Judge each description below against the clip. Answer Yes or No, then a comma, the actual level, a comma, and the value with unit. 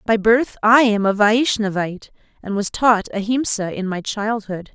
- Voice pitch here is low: No, high, 215 Hz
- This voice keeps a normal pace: Yes, average, 165 wpm